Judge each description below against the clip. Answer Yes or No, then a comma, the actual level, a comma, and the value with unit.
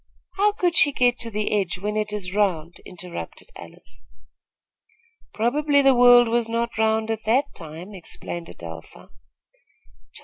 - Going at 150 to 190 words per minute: No, average, 140 wpm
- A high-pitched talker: Yes, high, 220 Hz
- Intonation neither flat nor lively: Yes, average, 4.8 semitones